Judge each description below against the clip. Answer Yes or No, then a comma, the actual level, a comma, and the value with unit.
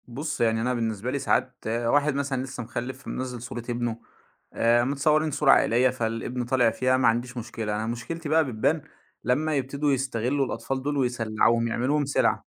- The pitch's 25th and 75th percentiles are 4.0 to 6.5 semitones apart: No, average, 2.9 semitones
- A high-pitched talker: No, low, 125 Hz